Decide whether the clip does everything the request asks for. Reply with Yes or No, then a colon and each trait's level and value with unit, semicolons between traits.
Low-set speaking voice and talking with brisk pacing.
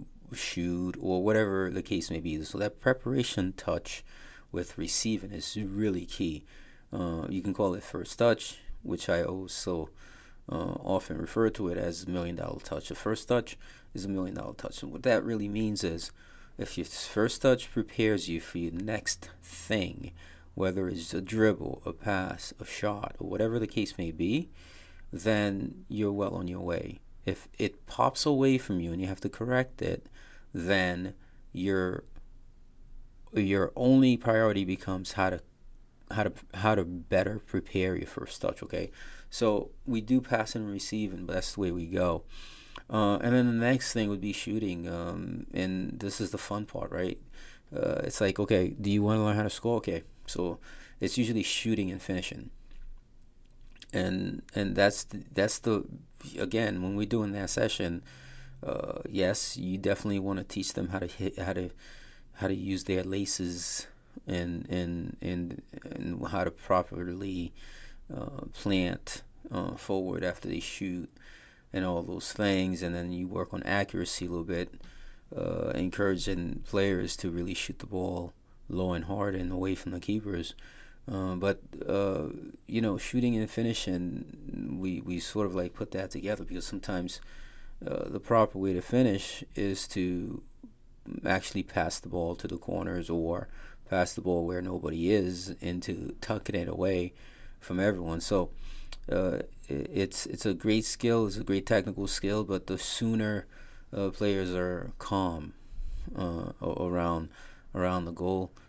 No: very low, 95 Hz; average, 165 wpm